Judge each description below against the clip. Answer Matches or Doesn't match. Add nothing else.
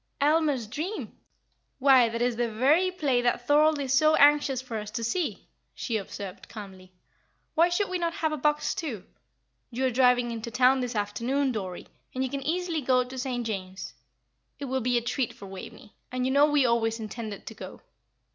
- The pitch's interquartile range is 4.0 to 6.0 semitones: Matches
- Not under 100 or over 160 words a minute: Doesn't match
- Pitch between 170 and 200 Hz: Doesn't match